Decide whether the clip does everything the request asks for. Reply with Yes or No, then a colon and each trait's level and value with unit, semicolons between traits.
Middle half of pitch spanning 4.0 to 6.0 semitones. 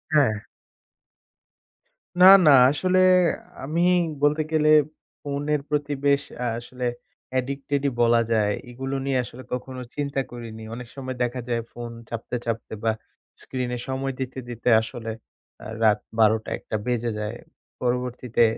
No: average, 3.0 semitones